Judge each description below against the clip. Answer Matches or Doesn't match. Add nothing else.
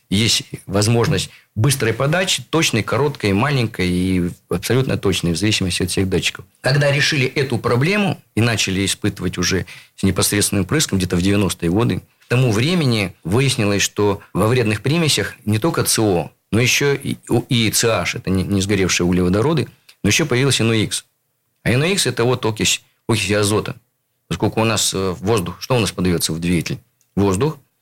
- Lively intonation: Doesn't match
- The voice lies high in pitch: Doesn't match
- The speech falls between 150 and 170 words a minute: Matches